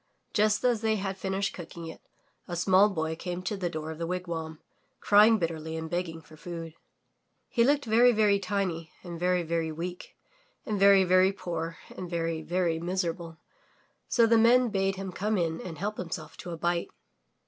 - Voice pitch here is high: No, medium, 180 Hz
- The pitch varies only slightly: No, average, 3.2 semitones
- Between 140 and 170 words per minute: No, average, 180 wpm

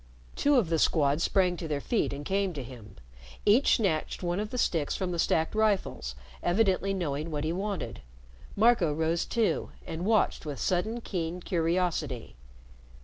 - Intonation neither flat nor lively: Yes, average, 4.5 semitones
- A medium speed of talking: Yes, average, 165 wpm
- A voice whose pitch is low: No, medium, 175 Hz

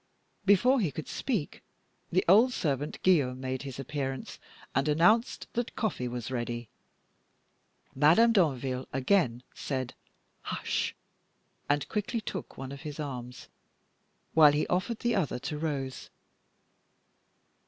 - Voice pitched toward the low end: No, medium, 145 Hz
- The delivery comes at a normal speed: No, slow, 120 wpm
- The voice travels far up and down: Yes, wide, 6.5 semitones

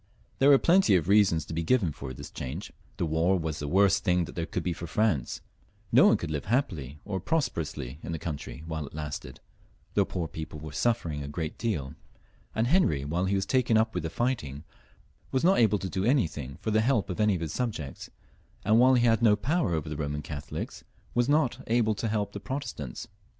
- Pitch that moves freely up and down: Yes, wide, 6.8 semitones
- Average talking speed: No, fast, 215 wpm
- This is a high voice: No, very low, 95 Hz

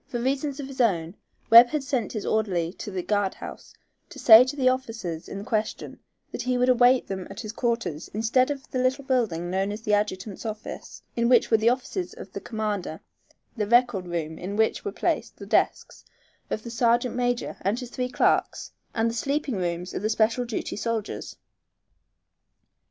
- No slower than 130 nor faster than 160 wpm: No, average, 190 wpm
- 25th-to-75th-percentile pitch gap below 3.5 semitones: No, average, 3.8 semitones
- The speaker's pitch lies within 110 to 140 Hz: No, high, 225 Hz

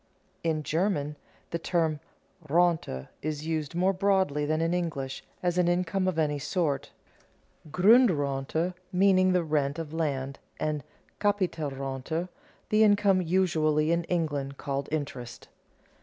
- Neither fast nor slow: No, slow, 125 wpm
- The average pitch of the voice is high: No, medium, 160 Hz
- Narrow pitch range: No, average, 3.8 semitones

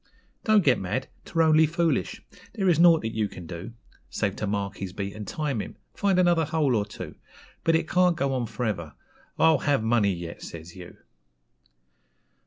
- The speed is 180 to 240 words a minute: Yes, average, 190 wpm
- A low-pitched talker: Yes, low, 125 Hz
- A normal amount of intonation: No, wide, 8.4 semitones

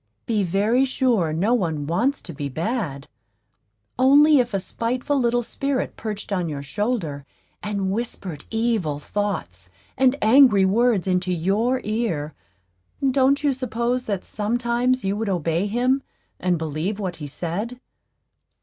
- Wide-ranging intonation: Yes, wide, 5.7 semitones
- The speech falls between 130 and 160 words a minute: Yes, average, 140 wpm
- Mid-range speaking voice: No, high, 210 Hz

